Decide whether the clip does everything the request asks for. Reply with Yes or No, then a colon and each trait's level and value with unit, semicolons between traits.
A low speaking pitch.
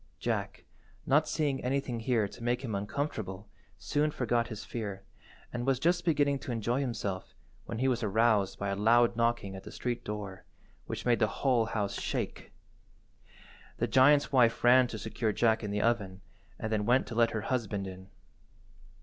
Yes: low, 115 Hz